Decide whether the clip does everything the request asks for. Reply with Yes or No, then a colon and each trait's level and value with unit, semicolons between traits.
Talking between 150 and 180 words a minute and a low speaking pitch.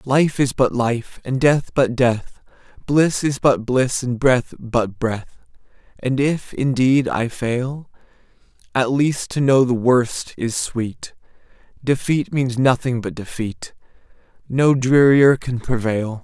No: average, 140 wpm; low, 125 Hz